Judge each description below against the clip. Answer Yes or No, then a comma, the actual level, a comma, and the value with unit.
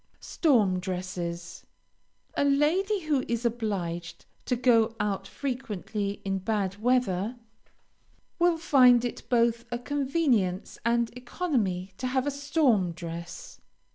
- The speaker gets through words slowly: Yes, slow, 115 wpm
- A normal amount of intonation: No, wide, 5.8 semitones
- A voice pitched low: No, high, 235 Hz